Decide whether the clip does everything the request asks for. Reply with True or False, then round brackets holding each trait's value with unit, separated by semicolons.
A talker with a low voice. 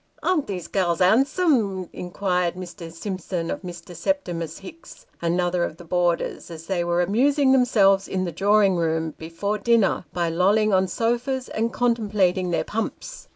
False (185 Hz)